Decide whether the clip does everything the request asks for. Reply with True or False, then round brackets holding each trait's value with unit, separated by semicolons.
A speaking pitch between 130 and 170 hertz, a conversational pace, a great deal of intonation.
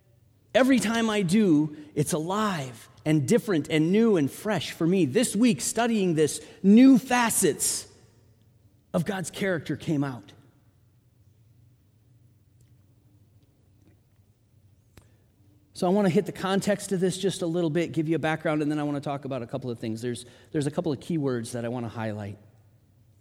True (140 Hz; 170 wpm; 8.0 semitones)